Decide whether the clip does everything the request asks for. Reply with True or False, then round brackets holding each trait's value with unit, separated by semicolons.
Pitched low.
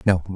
True (90 Hz)